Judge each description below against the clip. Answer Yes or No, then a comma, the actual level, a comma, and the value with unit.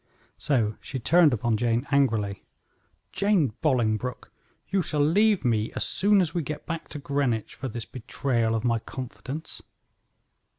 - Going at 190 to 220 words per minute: No, average, 145 wpm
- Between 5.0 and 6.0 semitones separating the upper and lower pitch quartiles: Yes, wide, 5.4 semitones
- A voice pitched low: Yes, low, 130 Hz